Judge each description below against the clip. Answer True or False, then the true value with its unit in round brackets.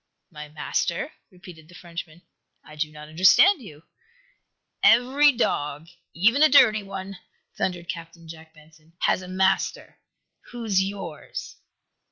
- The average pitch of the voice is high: False (175 Hz)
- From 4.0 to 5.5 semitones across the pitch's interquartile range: True (4.3 semitones)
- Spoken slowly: True (125 wpm)